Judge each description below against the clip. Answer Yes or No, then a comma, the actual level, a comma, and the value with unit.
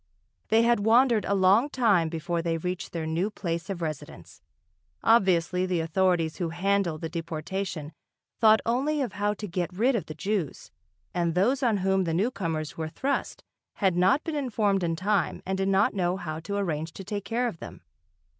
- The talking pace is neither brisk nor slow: Yes, average, 185 wpm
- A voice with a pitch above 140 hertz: Yes, high, 190 Hz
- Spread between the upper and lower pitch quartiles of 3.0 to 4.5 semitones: Yes, average, 4.1 semitones